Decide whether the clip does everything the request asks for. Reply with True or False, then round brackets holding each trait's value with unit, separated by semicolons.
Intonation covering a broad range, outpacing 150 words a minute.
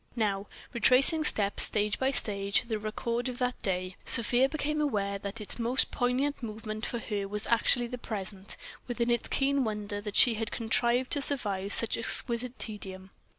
False (3.4 semitones; 165 wpm)